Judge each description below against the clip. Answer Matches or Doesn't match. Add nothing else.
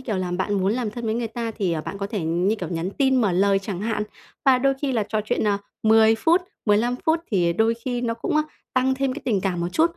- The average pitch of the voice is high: Matches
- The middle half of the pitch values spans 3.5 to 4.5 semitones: Matches